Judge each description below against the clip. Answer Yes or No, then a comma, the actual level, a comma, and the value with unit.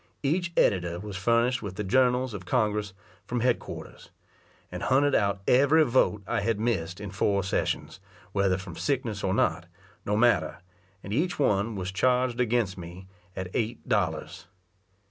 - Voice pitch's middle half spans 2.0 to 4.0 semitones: No, average, 4.5 semitones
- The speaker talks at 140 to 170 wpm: Yes, average, 160 wpm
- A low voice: Yes, low, 105 Hz